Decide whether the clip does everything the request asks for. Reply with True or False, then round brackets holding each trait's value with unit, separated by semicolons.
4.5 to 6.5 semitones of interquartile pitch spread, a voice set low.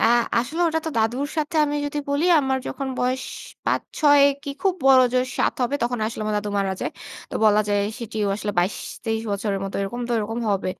False (5.2 semitones; 240 Hz)